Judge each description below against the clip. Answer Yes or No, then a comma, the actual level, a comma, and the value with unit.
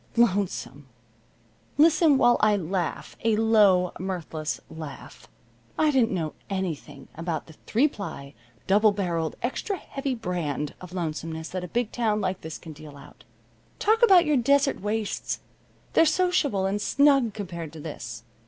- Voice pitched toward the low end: No, high, 195 Hz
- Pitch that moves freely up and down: Yes, wide, 6.9 semitones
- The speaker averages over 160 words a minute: No, average, 145 wpm